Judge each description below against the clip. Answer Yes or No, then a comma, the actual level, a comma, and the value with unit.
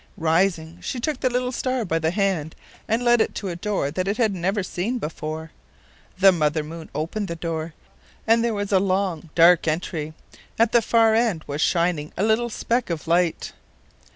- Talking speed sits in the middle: Yes, average, 190 wpm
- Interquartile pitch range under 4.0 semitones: No, average, 5.3 semitones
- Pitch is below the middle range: No, medium, 185 Hz